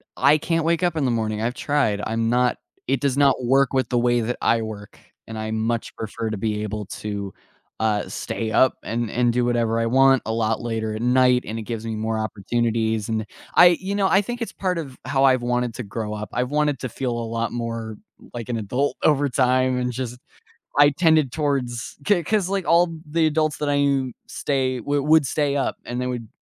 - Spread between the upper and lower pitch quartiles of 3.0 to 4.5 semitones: Yes, average, 4.1 semitones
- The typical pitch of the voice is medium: No, low, 125 Hz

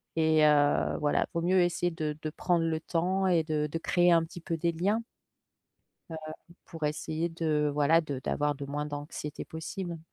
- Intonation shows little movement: Yes, narrow, 2.3 semitones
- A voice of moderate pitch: Yes, medium, 160 Hz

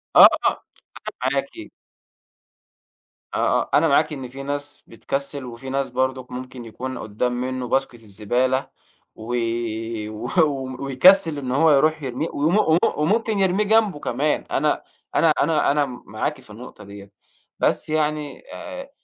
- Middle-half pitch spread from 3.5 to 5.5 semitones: Yes, average, 3.9 semitones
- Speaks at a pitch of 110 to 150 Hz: Yes, low, 135 Hz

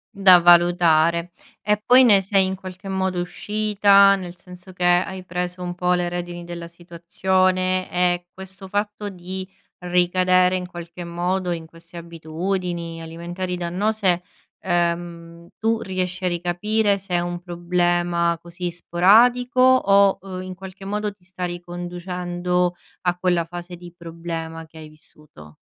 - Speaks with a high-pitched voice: No, medium, 180 Hz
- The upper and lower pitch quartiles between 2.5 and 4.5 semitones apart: No, narrow, 1.6 semitones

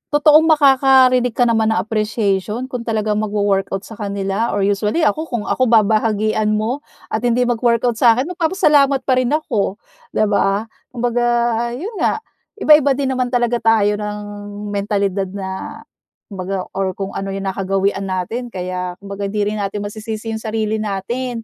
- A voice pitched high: Yes, high, 220 Hz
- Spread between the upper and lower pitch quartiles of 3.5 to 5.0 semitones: Yes, average, 3.8 semitones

